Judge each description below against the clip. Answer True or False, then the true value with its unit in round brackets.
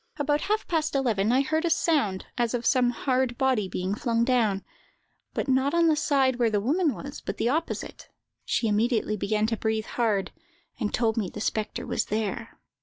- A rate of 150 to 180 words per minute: False (190 wpm)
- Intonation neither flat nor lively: True (4.3 semitones)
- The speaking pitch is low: False (240 Hz)